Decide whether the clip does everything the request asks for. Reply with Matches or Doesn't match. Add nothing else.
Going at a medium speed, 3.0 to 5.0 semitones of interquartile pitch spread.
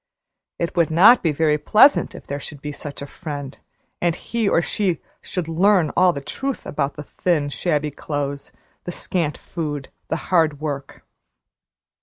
Matches